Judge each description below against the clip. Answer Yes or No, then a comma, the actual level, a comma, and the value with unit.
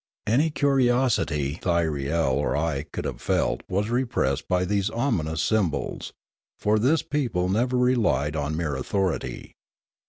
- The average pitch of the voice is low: Yes, very low, 95 Hz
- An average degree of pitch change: No, wide, 7.9 semitones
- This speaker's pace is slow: Yes, slow, 130 wpm